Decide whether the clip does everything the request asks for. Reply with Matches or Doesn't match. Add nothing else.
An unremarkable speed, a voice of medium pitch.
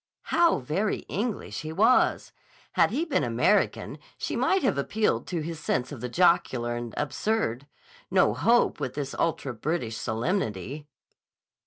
Matches